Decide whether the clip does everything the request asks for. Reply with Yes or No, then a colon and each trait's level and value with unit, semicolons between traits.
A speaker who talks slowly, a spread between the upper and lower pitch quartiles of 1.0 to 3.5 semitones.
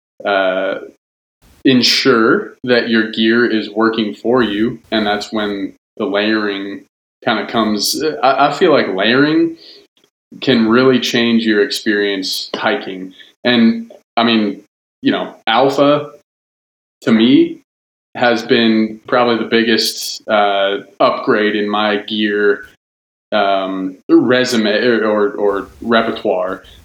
Yes: slow, 115 wpm; average, 2.7 semitones